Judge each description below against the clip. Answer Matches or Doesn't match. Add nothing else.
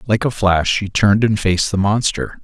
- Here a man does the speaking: Matches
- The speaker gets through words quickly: Matches